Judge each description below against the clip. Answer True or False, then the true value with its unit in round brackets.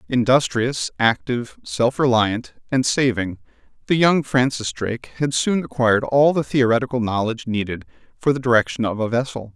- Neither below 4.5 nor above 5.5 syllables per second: True (5.2 syllables/s)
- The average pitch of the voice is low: True (120 Hz)